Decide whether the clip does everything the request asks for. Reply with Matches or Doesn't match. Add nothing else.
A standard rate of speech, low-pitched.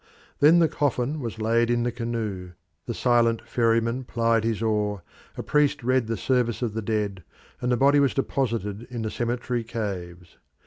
Matches